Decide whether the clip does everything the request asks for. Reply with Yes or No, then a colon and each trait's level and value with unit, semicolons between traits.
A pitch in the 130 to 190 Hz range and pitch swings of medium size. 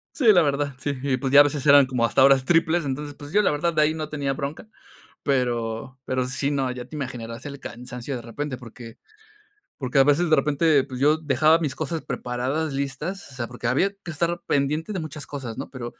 Yes: medium, 140 Hz; average, 3.2 semitones